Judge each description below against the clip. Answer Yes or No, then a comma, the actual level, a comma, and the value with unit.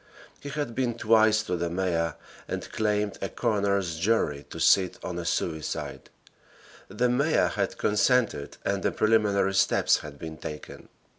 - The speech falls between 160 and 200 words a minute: No, average, 150 wpm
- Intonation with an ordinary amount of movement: Yes, average, 4.8 semitones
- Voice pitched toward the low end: Yes, low, 100 Hz